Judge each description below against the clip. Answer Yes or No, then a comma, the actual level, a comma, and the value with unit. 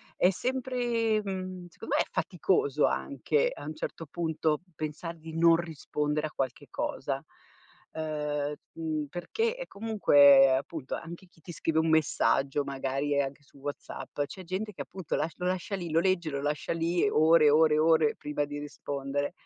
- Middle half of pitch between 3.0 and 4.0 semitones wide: Yes, average, 3.7 semitones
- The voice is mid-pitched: Yes, medium, 160 Hz